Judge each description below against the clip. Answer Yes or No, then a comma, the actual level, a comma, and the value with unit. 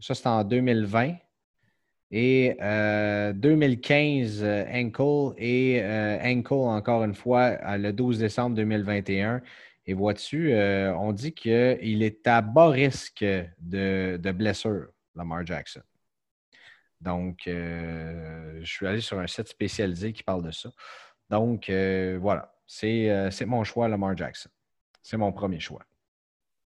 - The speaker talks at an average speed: No, slow, 140 wpm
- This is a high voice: No, low, 105 Hz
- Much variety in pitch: No, average, 4.1 semitones